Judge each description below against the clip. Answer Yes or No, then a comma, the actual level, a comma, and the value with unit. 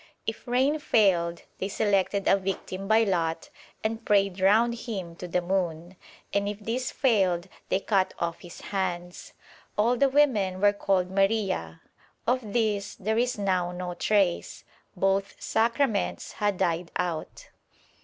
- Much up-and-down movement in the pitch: No, average, 3.5 semitones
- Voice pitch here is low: No, high, 195 Hz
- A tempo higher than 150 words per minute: No, average, 145 wpm